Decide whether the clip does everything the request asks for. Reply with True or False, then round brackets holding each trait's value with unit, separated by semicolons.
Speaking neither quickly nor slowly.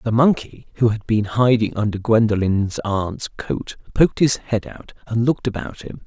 True (180 wpm)